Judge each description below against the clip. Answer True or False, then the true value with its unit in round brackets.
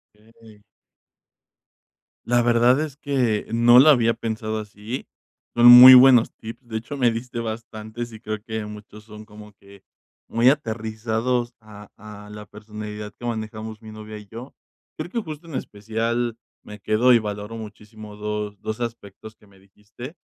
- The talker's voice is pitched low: True (110 Hz)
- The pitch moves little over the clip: True (2.1 semitones)